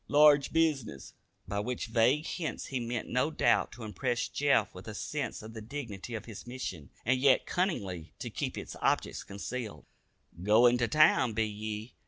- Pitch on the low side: Yes, low, 120 Hz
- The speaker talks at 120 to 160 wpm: No, average, 175 wpm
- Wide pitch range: No, average, 4.4 semitones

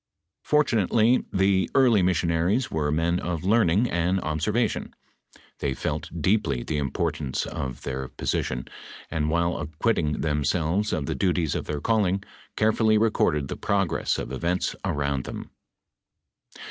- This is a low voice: Yes, very low, 85 Hz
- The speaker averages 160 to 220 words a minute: No, slow, 135 wpm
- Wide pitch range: Yes, wide, 5.7 semitones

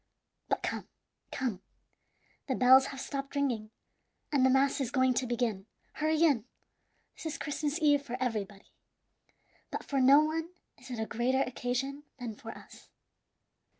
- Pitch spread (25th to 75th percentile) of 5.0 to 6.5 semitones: No, average, 2.8 semitones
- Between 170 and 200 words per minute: No, average, 150 wpm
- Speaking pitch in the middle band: No, very high, 260 Hz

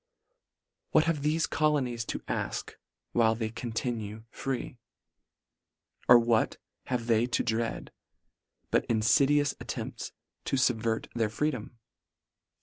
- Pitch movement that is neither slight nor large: Yes, average, 3.6 semitones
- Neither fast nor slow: No, slow, 110 wpm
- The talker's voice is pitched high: No, low, 120 Hz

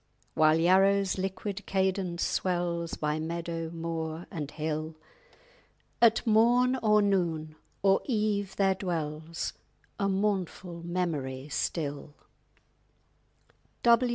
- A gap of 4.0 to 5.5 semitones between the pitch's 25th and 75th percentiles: No, average, 3.6 semitones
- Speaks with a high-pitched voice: No, medium, 175 Hz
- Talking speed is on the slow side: Yes, slow, 100 wpm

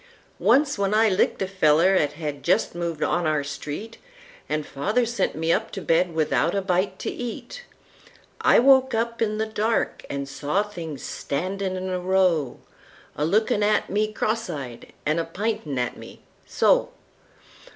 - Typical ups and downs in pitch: No, wide, 5.8 semitones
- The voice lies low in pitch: No, medium, 185 Hz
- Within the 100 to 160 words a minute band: Yes, average, 150 wpm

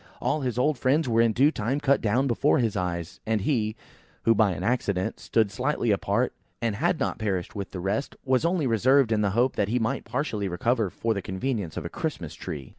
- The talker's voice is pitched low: Yes, low, 115 Hz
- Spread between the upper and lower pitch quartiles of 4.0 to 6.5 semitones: Yes, average, 4.6 semitones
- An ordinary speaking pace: No, fast, 220 wpm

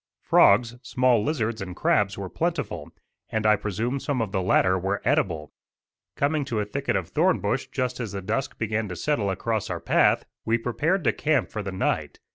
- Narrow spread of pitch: No, average, 4.4 semitones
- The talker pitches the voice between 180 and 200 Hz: No, low, 110 Hz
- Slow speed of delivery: No, average, 195 wpm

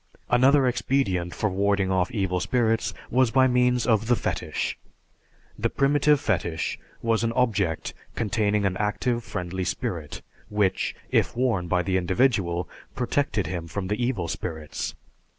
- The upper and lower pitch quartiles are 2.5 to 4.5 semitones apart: No, average, 5.2 semitones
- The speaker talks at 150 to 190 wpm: No, average, 140 wpm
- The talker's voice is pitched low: Yes, low, 105 Hz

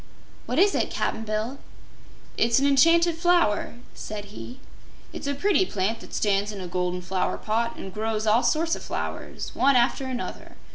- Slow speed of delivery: No, average, 175 wpm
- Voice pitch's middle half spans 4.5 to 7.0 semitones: Yes, average, 5.3 semitones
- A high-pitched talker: Yes, high, 230 Hz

